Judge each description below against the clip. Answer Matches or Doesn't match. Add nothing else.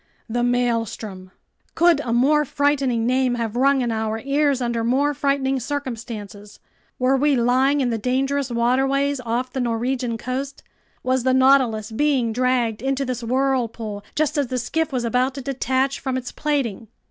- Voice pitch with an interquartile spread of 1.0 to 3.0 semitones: Matches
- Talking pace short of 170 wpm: Matches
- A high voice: Matches